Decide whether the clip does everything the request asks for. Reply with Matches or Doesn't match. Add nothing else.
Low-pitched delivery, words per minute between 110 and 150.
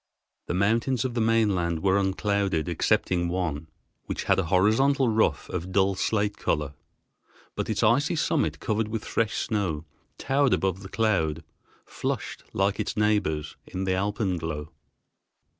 Matches